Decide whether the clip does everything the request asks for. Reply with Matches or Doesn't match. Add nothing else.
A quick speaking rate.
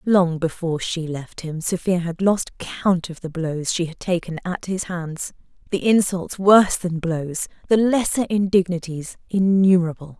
Doesn't match